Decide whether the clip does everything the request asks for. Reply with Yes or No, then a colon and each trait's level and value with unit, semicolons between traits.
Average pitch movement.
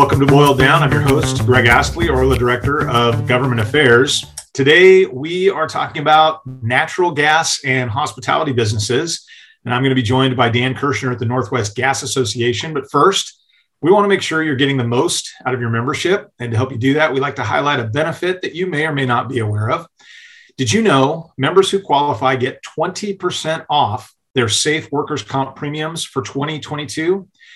Yes: average, 3.8 semitones